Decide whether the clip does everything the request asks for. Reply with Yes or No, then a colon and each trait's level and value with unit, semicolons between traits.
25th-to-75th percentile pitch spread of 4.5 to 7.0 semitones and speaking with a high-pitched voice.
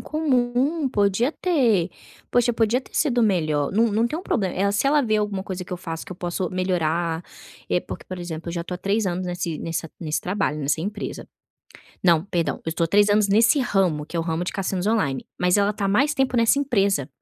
Yes: average, 5.0 semitones; high, 195 Hz